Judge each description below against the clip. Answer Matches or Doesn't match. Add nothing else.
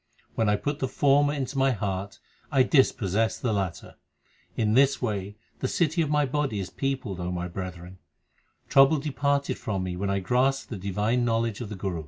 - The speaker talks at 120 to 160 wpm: Doesn't match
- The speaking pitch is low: Matches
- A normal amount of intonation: Doesn't match